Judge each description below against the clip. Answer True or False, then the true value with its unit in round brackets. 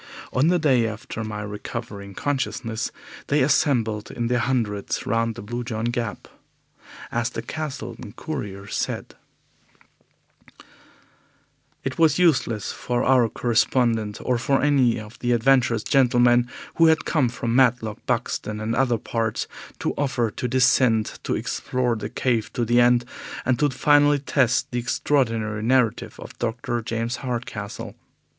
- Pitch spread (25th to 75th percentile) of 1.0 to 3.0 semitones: True (2.6 semitones)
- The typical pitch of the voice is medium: False (120 Hz)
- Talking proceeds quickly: False (140 wpm)